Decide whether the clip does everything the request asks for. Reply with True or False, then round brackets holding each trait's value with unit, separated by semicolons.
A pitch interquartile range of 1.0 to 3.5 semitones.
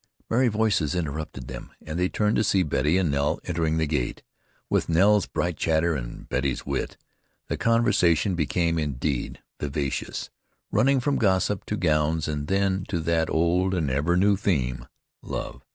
False (4.4 semitones)